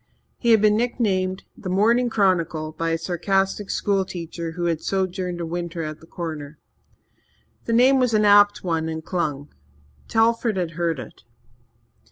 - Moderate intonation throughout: Yes, average, 4.0 semitones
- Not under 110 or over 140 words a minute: No, average, 155 wpm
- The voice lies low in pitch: No, medium, 185 Hz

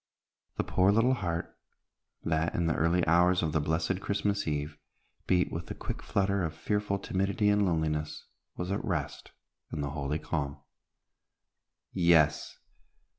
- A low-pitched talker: Yes, very low, 85 Hz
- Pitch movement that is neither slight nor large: Yes, average, 4.0 semitones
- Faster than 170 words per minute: No, average, 145 wpm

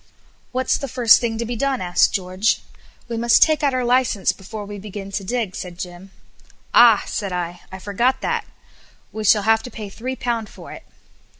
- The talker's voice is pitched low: No, high, 220 Hz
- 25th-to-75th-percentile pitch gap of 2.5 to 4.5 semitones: Yes, average, 3.9 semitones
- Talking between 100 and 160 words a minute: No, average, 195 wpm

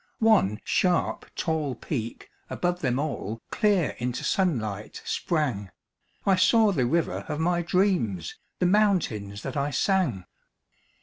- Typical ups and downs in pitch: No, wide, 8.1 semitones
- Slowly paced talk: Yes, slow, 125 wpm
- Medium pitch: Yes, medium, 155 Hz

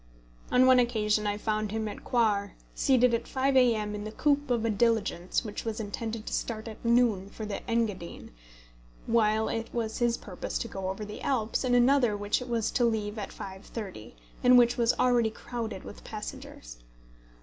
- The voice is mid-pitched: No, high, 225 Hz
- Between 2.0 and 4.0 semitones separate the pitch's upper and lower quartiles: Yes, narrow, 2.4 semitones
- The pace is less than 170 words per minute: No, average, 185 wpm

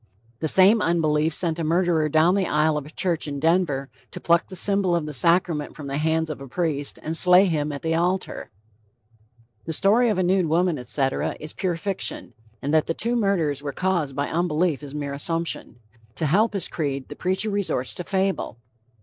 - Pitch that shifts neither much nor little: Yes, average, 3.6 semitones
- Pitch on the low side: No, medium, 165 Hz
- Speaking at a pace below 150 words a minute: No, average, 200 wpm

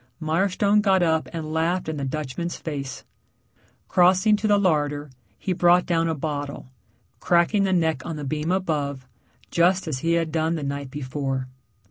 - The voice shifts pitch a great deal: No, average, 3.6 semitones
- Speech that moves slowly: No, average, 165 wpm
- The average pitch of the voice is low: No, medium, 160 Hz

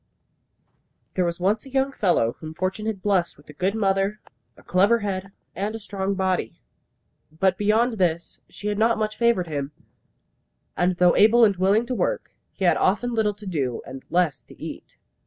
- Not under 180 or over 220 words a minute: Yes, average, 185 wpm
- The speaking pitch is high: Yes, high, 195 Hz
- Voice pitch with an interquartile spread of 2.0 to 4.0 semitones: Yes, average, 3.4 semitones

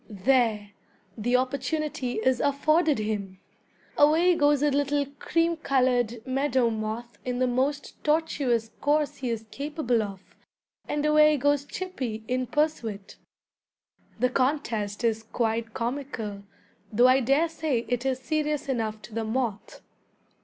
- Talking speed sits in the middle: No, slow, 130 wpm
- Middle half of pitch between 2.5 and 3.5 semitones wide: No, average, 4.4 semitones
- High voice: Yes, very high, 255 Hz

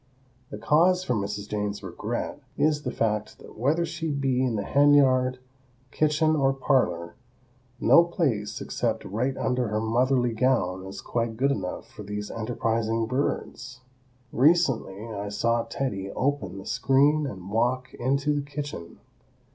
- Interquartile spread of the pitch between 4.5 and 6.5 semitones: Yes, average, 4.9 semitones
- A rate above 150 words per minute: No, average, 145 wpm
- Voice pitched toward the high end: No, low, 125 Hz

